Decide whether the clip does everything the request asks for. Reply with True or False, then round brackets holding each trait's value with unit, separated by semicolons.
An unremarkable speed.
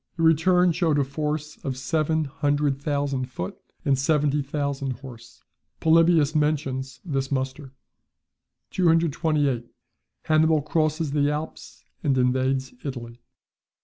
False (115 wpm)